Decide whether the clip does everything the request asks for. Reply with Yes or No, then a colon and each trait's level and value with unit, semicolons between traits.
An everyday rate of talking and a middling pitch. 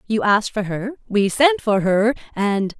No: average, 195 wpm; high, 215 Hz